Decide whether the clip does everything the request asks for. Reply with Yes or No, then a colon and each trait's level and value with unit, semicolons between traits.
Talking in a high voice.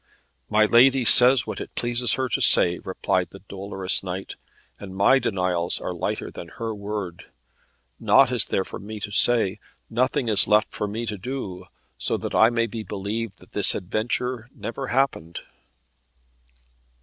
No: low, 105 Hz